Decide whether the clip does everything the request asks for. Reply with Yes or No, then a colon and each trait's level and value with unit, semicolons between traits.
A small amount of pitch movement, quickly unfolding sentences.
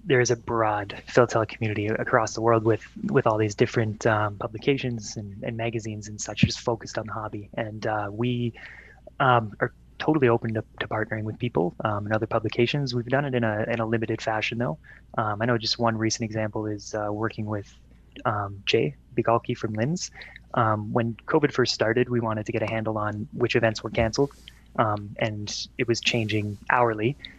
No: narrow, 2.0 semitones; average, 195 wpm